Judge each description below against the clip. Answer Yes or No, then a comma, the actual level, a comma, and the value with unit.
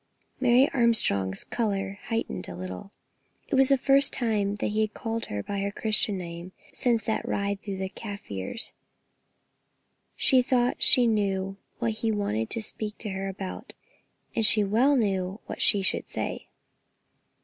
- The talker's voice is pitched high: Yes, high, 210 Hz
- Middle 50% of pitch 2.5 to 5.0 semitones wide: Yes, average, 3.2 semitones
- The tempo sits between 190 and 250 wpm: No, average, 155 wpm